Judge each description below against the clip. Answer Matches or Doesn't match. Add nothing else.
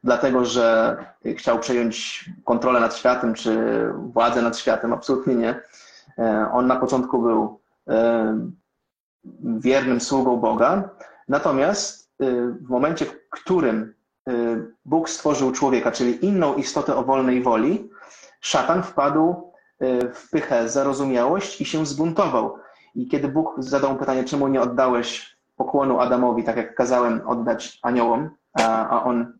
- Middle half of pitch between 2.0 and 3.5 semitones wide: Matches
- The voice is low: Matches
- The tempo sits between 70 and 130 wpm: Matches